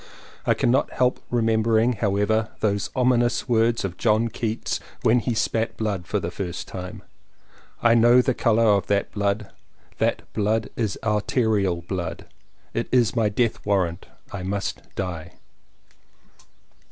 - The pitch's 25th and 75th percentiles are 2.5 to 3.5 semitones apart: Yes, average, 2.9 semitones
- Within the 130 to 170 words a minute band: Yes, average, 140 wpm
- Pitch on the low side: Yes, low, 110 Hz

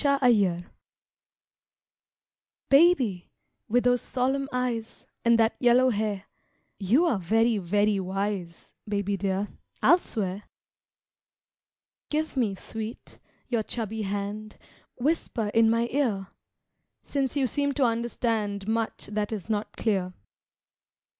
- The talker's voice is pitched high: Yes, high, 220 Hz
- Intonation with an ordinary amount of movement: Yes, average, 3.6 semitones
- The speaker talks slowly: Yes, slow, 115 wpm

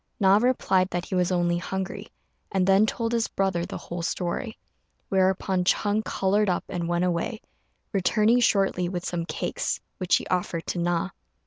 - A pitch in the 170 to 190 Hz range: Yes, medium, 185 Hz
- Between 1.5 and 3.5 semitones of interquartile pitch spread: Yes, narrow, 2.5 semitones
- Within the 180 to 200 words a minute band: No, average, 165 wpm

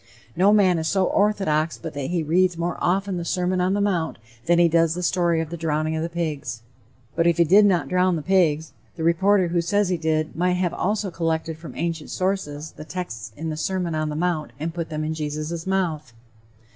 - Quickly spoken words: Yes, fast, 220 wpm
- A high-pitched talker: No, medium, 170 Hz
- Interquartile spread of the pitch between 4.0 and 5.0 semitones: No, narrow, 2.5 semitones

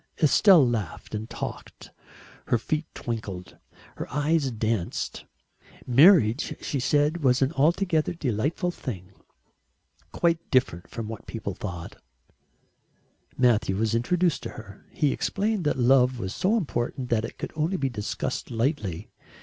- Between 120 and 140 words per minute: Yes, slow, 135 wpm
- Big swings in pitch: Yes, wide, 6.0 semitones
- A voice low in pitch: Yes, low, 130 Hz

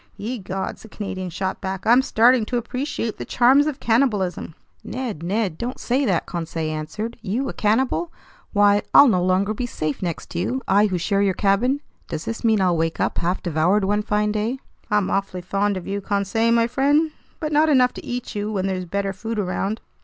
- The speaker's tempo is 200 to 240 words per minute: Yes, fast, 205 wpm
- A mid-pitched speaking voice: No, high, 205 Hz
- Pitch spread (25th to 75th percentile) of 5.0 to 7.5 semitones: No, average, 4.3 semitones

